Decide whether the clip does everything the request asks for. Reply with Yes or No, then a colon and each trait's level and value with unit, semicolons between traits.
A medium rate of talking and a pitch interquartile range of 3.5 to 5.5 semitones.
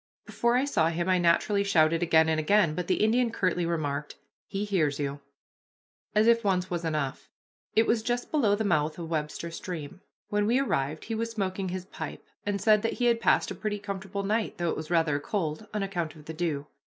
No: fast, 215 wpm; average, 4.8 semitones